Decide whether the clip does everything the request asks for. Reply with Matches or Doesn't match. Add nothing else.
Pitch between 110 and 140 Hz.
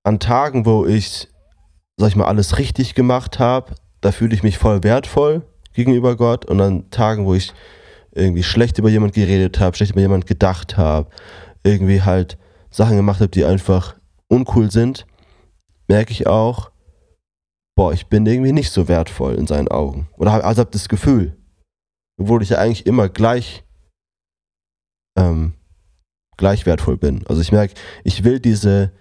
Doesn't match